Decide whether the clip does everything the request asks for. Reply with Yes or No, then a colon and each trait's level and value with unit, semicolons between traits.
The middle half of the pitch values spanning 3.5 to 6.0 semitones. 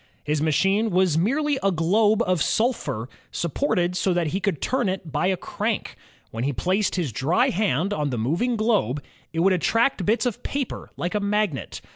Yes: average, 5.0 semitones